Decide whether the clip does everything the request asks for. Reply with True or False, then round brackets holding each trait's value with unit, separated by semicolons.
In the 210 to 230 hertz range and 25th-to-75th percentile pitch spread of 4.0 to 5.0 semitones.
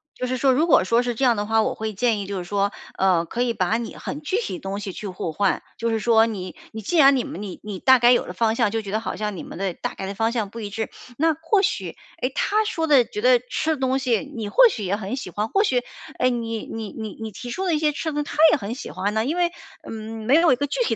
True (225 Hz; 4.4 semitones)